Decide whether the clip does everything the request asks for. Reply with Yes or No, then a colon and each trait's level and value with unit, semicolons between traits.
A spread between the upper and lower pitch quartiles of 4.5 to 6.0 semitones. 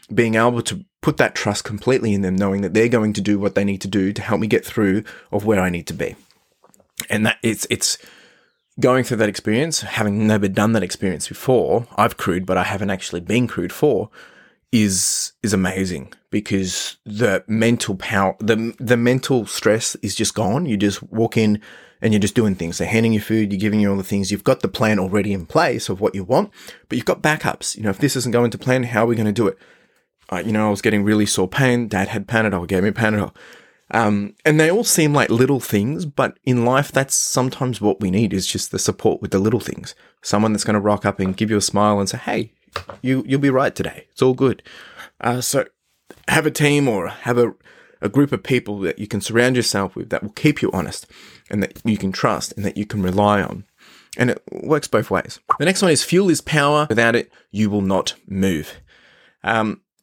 No: average, 3.4 semitones